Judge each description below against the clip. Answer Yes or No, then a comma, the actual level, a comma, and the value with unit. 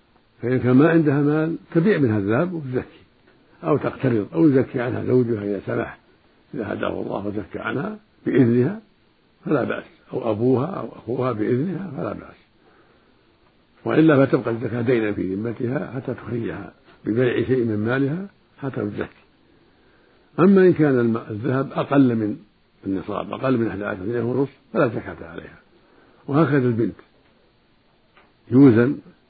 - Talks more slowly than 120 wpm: No, average, 130 wpm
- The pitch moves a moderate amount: Yes, average, 3.8 semitones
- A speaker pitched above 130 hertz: No, low, 125 Hz